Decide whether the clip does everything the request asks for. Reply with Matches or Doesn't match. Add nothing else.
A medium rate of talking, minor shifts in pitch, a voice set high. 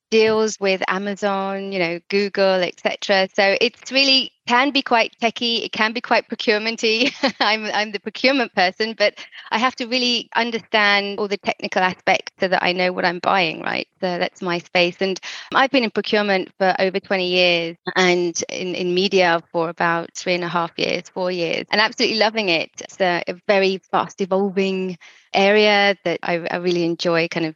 Doesn't match